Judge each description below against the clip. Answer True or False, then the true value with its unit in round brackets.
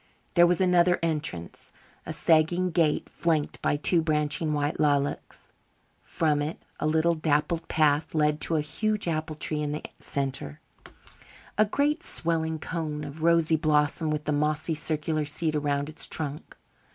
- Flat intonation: True (1.9 semitones)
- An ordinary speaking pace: True (150 wpm)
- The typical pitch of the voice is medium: True (155 Hz)